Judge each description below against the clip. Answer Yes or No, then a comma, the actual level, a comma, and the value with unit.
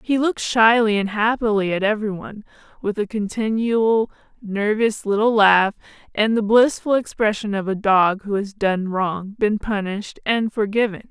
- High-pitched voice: Yes, high, 210 Hz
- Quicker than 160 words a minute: No, average, 155 wpm